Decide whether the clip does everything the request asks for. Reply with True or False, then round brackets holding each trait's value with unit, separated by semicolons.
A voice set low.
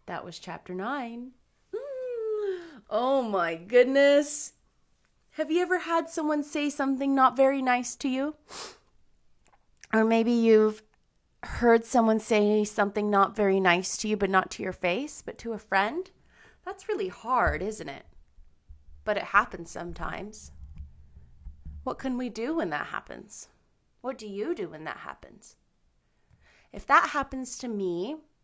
False (225 Hz)